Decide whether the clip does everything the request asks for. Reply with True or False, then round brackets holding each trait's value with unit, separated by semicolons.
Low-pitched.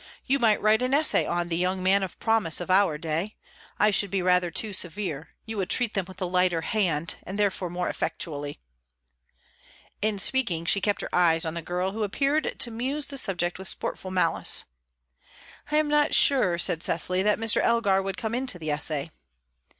False (190 Hz)